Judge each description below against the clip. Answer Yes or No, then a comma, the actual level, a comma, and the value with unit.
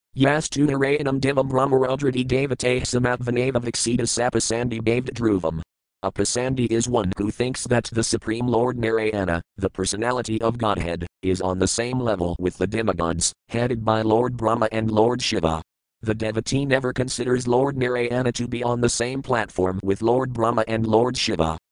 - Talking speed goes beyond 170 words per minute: No, average, 160 wpm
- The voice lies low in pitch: Yes, low, 115 Hz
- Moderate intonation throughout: Yes, average, 3.3 semitones